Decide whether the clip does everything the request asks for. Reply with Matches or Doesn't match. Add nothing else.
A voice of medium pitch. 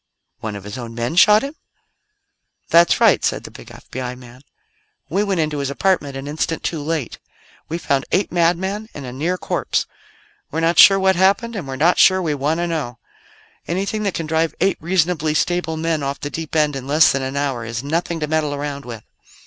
Matches